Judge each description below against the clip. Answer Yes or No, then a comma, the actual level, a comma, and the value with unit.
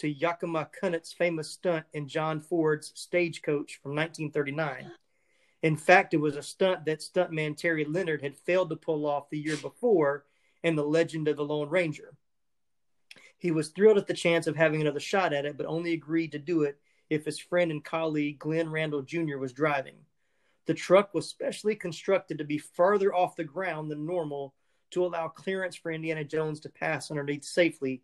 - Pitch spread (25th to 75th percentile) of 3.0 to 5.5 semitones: No, narrow, 2.6 semitones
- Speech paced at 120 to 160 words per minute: No, average, 185 wpm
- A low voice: No, medium, 160 Hz